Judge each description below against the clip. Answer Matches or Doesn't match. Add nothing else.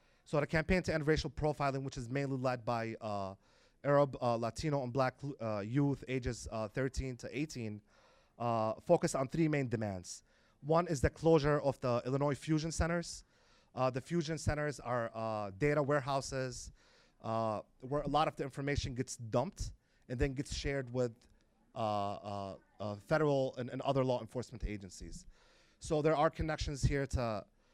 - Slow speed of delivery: Doesn't match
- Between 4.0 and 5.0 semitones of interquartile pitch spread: Matches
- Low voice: Matches